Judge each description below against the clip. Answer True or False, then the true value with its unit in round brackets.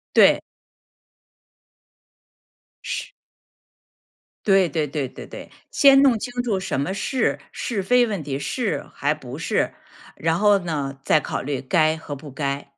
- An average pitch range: False (6.6 semitones)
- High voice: False (160 Hz)